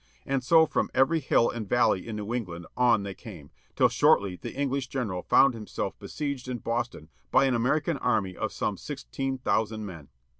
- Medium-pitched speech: No, low, 120 Hz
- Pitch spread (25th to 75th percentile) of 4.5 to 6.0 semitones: Yes, average, 4.9 semitones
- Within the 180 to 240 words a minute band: Yes, average, 185 wpm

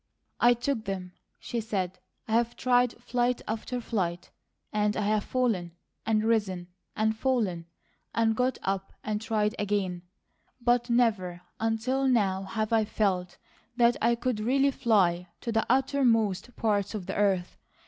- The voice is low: No, high, 220 Hz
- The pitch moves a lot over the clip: No, average, 3.6 semitones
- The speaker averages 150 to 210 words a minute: No, average, 140 wpm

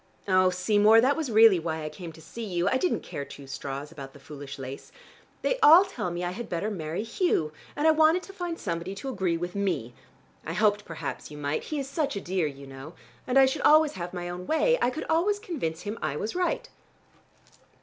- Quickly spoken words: Yes, fast, 225 wpm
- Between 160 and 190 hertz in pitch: Yes, medium, 185 Hz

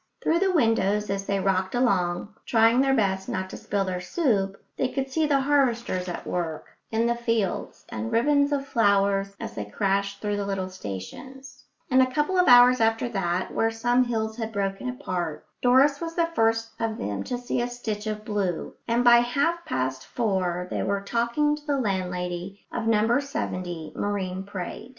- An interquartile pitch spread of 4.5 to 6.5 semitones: Yes, average, 4.8 semitones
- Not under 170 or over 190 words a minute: Yes, average, 185 wpm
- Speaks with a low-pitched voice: No, high, 220 Hz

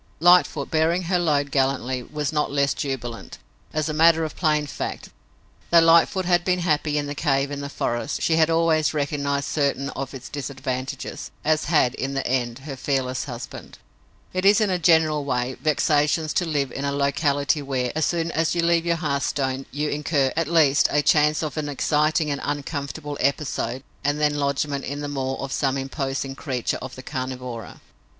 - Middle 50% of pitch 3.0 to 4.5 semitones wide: No, narrow, 2.5 semitones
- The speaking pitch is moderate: Yes, medium, 145 Hz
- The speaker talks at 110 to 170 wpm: No, average, 185 wpm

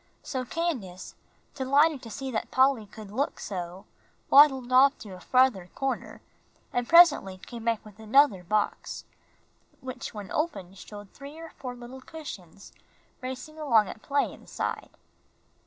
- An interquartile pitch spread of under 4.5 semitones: No, average, 5.0 semitones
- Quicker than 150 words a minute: No, average, 140 wpm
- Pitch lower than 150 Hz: No, very high, 250 Hz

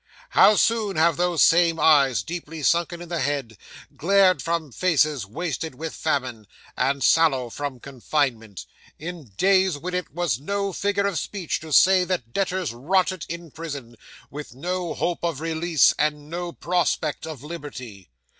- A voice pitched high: No, medium, 160 Hz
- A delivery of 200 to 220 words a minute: No, average, 155 wpm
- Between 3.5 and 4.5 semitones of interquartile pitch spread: Yes, average, 4.0 semitones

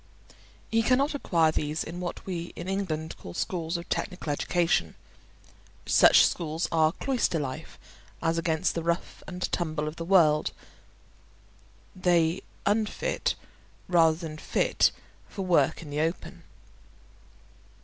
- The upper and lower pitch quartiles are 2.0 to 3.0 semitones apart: Yes, average, 2.7 semitones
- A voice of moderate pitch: Yes, medium, 170 Hz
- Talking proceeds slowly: Yes, slow, 130 wpm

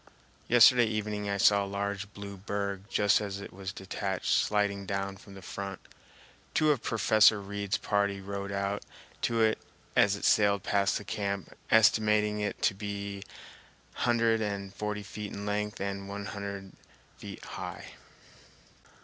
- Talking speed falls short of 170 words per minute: Yes, average, 155 wpm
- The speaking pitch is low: Yes, low, 100 Hz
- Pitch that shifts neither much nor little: No, narrow, 1.0 semitones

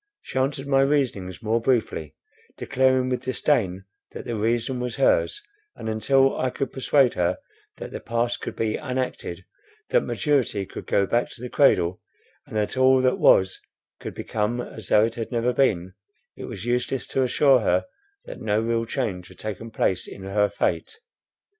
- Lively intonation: No, average, 3.7 semitones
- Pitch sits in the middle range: No, low, 120 Hz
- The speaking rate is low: No, average, 175 wpm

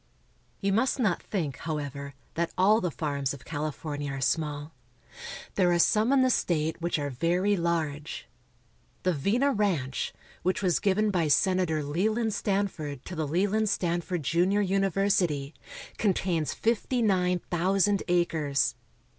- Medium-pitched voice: Yes, medium, 175 Hz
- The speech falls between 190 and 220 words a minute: No, average, 145 wpm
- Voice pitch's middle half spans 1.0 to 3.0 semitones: No, average, 4.7 semitones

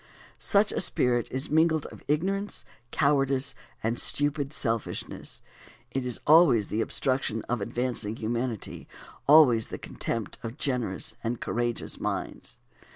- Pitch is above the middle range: No, low, 130 Hz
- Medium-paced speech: No, slow, 125 wpm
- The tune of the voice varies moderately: Yes, average, 4.2 semitones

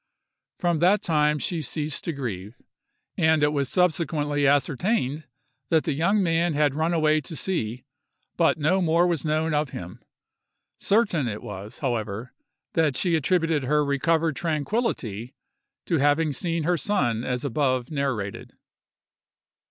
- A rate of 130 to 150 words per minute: Yes, average, 140 wpm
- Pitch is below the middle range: No, medium, 150 Hz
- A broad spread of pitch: No, average, 3.8 semitones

